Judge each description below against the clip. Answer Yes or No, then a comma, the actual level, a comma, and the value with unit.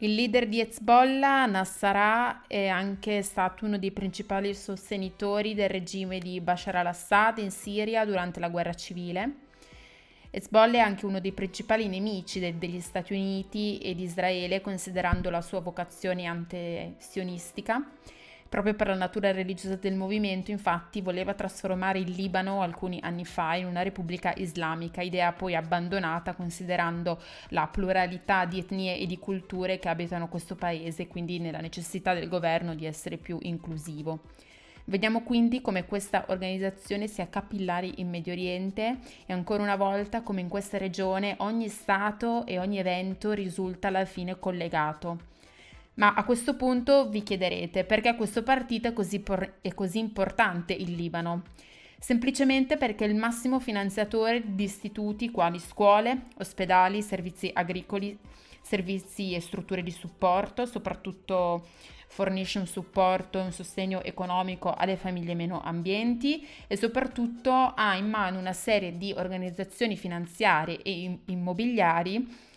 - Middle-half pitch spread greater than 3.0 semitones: No, narrow, 2.6 semitones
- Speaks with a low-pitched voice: No, high, 190 Hz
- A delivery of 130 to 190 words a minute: Yes, average, 140 wpm